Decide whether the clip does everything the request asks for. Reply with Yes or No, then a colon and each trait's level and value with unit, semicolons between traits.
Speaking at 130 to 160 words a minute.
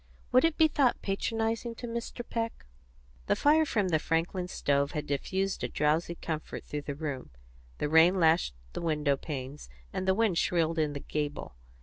No: average, 170 wpm